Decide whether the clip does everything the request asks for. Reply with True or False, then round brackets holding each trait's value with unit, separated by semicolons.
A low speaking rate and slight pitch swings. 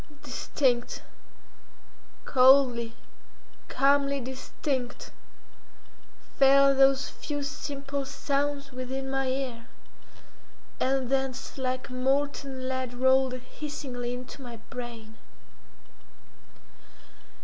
True (75 wpm; 1.5 semitones)